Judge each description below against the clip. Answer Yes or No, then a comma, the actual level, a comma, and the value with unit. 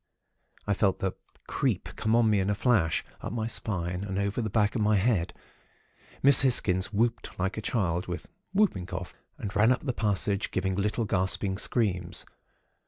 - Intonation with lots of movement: No, average, 3.0 semitones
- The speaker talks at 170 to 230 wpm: Yes, average, 175 wpm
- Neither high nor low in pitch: No, low, 105 Hz